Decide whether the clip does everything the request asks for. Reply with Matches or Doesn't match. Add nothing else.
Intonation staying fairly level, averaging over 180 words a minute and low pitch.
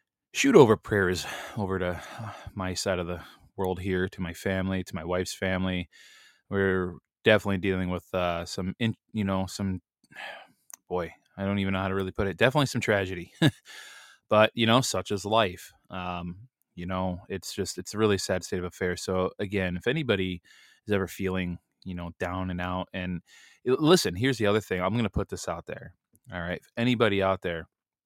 Matches